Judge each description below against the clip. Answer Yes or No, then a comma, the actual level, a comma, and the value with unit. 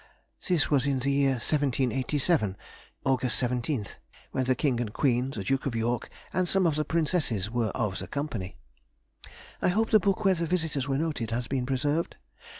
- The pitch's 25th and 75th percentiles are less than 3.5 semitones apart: No, average, 4.3 semitones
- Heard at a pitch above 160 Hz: No, low, 135 Hz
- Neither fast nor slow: Yes, average, 180 wpm